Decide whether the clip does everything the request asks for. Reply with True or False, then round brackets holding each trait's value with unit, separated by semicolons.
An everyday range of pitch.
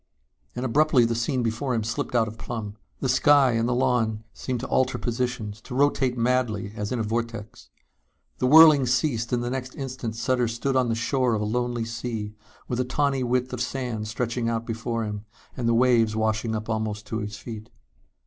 False (2.3 semitones)